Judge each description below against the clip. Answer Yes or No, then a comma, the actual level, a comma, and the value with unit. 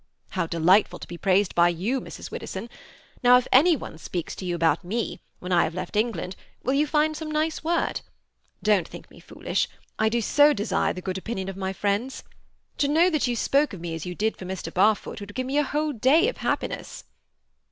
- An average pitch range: No, wide, 7.4 semitones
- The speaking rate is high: Yes, fast, 215 wpm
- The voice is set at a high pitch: Yes, high, 215 Hz